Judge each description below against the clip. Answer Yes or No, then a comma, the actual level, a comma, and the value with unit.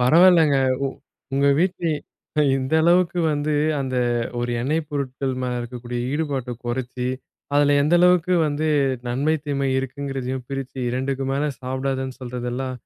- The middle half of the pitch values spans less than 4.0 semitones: Yes, average, 2.9 semitones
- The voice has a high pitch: No, low, 135 Hz